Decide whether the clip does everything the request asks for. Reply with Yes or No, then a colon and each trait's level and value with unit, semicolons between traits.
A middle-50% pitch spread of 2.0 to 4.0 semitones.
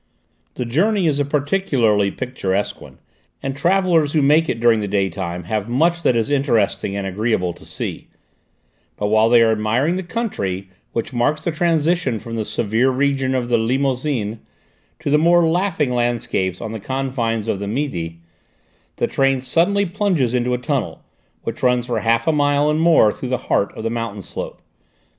No: wide, 5.4 semitones